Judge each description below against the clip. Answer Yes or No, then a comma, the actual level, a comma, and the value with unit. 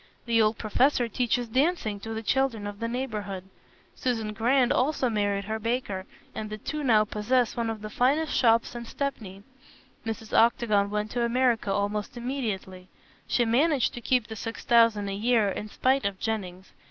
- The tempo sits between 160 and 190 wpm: Yes, average, 175 wpm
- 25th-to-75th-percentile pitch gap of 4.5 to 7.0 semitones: No, average, 3.0 semitones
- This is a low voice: No, high, 225 Hz